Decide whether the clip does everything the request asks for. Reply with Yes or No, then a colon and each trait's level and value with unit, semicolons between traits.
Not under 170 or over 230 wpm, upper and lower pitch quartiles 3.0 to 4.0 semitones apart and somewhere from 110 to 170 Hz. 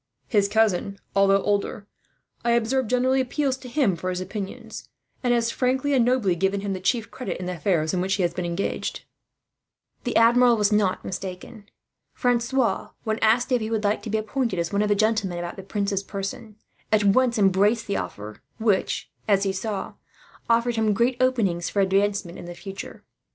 No: average, 190 wpm; average, 3.5 semitones; high, 210 Hz